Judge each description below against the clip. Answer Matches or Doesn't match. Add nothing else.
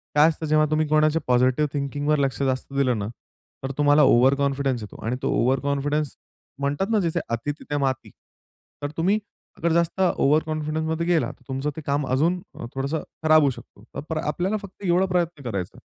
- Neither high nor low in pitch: Matches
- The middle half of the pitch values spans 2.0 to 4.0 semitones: Matches